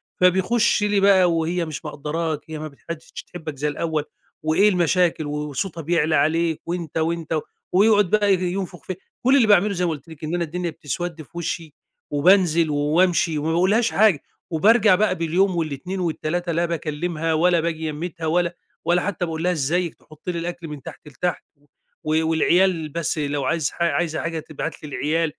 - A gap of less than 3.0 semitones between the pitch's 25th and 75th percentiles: Yes, narrow, 2.5 semitones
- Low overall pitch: No, medium, 170 Hz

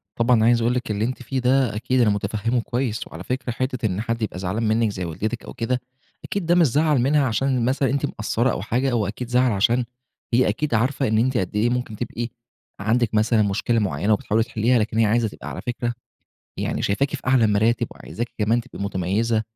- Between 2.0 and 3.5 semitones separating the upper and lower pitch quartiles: Yes, average, 2.8 semitones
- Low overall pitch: Yes, low, 115 Hz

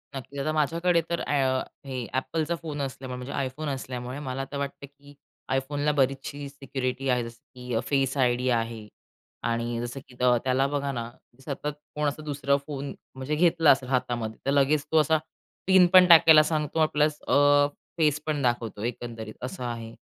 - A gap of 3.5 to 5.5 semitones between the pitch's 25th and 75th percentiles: No, average, 2.9 semitones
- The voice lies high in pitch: No, medium, 140 Hz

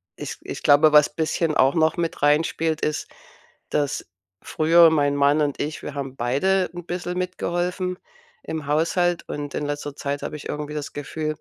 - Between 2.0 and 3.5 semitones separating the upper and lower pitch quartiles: Yes, average, 2.7 semitones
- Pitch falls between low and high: Yes, medium, 155 Hz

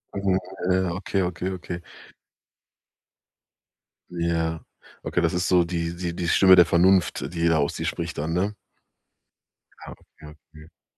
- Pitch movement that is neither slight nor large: No, narrow, 1.9 semitones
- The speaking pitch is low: Yes, very low, 85 Hz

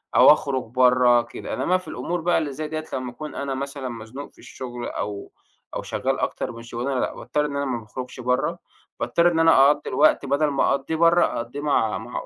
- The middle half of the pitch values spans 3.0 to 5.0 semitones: Yes, average, 3.6 semitones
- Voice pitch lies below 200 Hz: Yes, low, 135 Hz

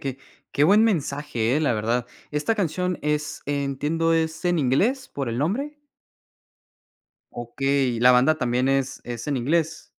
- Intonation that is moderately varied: Yes, average, 4.5 semitones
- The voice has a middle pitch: Yes, medium, 145 Hz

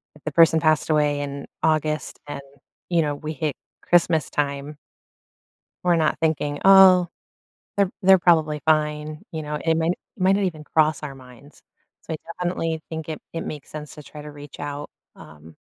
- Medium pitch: Yes, medium, 155 Hz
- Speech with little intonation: Yes, narrow, 1.9 semitones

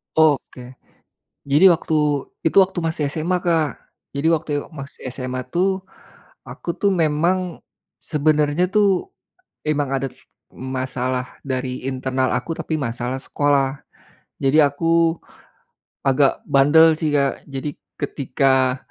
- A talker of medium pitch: Yes, medium, 145 Hz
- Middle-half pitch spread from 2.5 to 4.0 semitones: Yes, average, 3.6 semitones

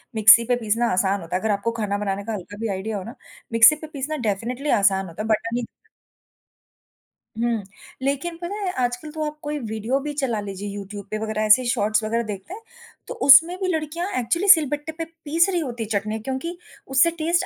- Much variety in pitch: Yes, wide, 6.3 semitones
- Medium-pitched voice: No, high, 235 Hz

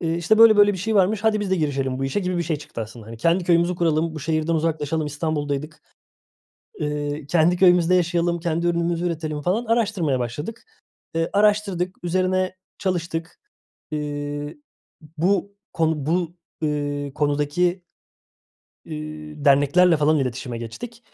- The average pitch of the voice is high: No, medium, 165 Hz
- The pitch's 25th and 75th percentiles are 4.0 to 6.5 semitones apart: No, average, 3.5 semitones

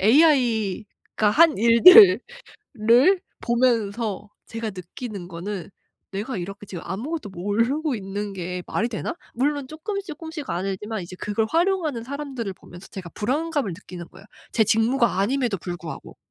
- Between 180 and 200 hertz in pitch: No, high, 225 Hz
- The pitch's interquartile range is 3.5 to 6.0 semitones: No, wide, 6.4 semitones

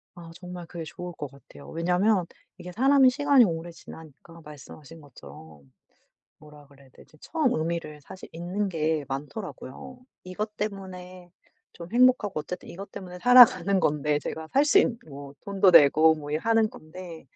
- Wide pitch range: No, average, 4.8 semitones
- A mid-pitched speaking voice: Yes, medium, 170 Hz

